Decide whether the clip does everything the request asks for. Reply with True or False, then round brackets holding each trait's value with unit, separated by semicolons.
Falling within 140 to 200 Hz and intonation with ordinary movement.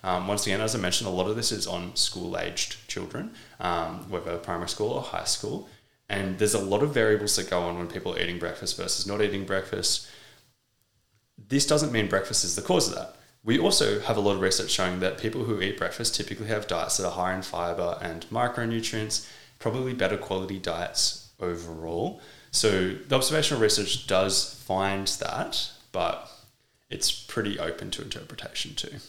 False (100 Hz; 3.1 semitones)